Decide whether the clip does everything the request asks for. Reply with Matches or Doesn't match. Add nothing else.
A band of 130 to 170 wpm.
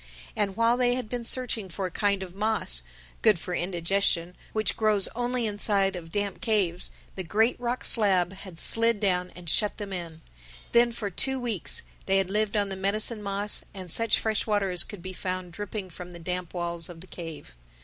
Doesn't match